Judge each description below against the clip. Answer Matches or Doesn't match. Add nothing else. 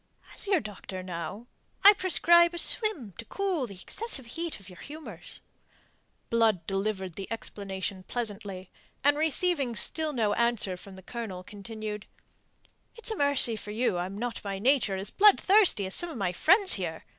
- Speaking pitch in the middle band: Doesn't match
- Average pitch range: Doesn't match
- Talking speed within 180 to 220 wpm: Doesn't match